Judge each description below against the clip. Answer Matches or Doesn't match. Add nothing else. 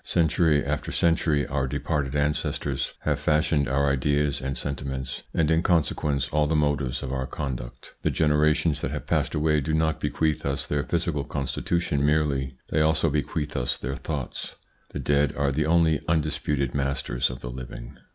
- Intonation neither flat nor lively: Doesn't match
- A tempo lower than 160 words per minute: Doesn't match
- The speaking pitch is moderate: Doesn't match